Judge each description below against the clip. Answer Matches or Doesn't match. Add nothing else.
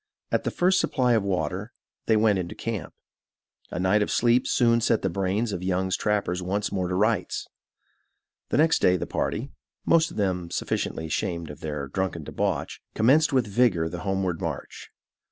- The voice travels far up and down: Doesn't match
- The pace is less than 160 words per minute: Doesn't match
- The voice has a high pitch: Doesn't match